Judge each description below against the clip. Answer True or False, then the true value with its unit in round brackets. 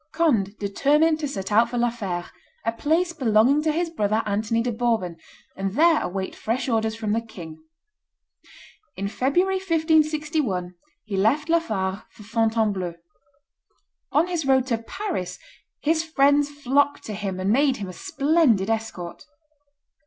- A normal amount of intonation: False (6.9 semitones)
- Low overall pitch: False (235 Hz)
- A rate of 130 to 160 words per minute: True (150 wpm)